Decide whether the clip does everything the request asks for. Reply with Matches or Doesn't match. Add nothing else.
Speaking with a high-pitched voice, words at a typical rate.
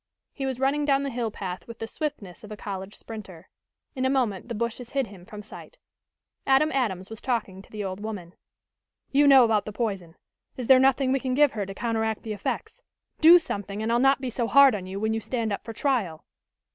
Doesn't match